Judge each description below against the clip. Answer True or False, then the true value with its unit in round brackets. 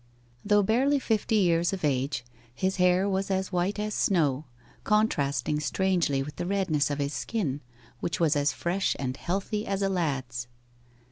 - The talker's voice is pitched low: False (175 Hz)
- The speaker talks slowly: False (160 wpm)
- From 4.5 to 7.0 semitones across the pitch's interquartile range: True (5.5 semitones)